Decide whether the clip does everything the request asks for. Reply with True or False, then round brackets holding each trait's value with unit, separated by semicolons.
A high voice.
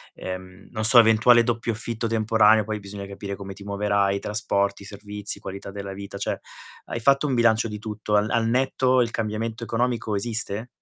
False (110 Hz)